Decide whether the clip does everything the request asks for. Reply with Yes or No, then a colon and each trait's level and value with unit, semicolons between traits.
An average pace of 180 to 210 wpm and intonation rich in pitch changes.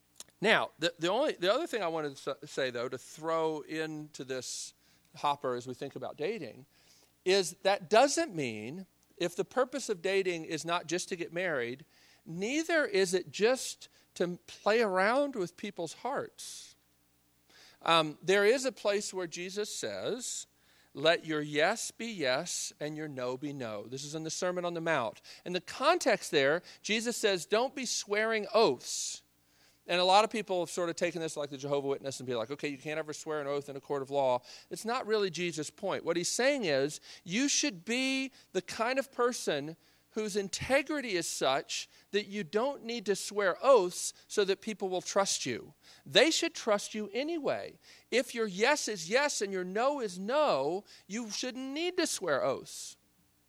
Yes: average, 185 wpm; wide, 6.7 semitones